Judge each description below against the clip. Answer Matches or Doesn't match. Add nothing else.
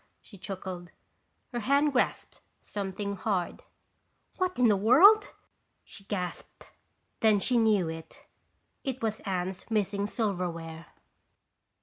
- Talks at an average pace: Doesn't match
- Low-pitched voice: Doesn't match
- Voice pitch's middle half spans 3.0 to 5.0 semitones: Matches